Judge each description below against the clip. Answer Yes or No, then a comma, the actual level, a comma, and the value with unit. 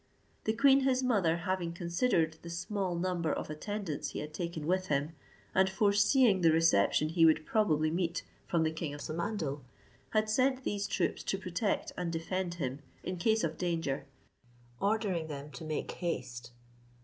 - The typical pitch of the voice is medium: Yes, medium, 170 Hz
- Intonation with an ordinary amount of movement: Yes, average, 4.3 semitones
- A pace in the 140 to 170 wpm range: Yes, average, 165 wpm